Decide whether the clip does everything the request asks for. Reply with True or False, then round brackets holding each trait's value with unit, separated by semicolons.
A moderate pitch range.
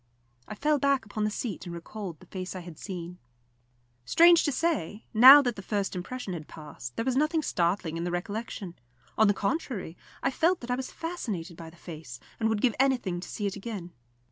False (6.5 semitones)